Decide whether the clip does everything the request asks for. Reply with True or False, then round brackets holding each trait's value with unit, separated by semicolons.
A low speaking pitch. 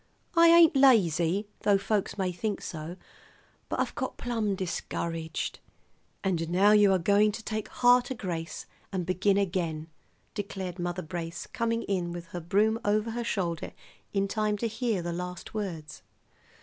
False (195 Hz)